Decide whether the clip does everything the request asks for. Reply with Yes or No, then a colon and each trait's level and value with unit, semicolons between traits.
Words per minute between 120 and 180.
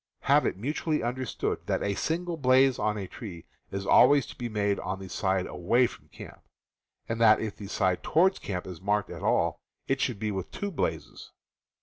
No: average, 200 wpm